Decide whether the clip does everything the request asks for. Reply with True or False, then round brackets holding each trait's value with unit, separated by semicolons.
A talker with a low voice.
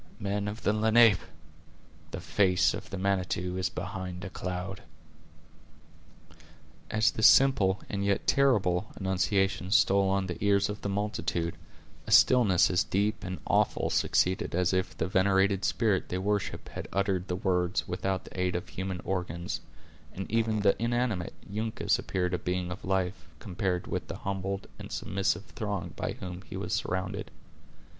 True (95 Hz)